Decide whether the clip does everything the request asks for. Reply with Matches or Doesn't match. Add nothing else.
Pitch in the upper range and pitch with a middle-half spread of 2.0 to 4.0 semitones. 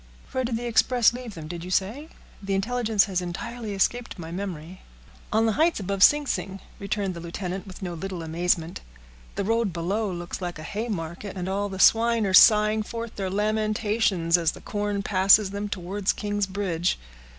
Matches